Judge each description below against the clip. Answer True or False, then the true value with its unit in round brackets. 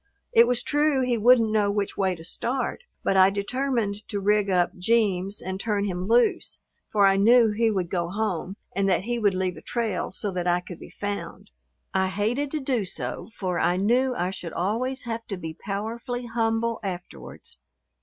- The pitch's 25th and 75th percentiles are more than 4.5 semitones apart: False (3.8 semitones)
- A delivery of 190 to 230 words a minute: True (195 wpm)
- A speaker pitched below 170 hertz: False (205 Hz)